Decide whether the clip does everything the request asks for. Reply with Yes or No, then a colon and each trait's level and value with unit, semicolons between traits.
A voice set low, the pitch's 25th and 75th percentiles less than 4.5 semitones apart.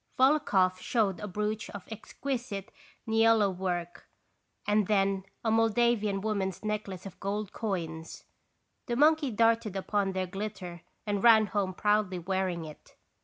No: high, 205 Hz; average, 2.8 semitones